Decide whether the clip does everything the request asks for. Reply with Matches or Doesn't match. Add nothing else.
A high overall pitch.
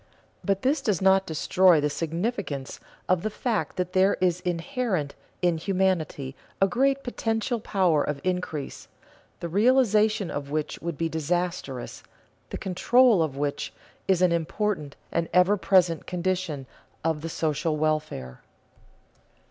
Doesn't match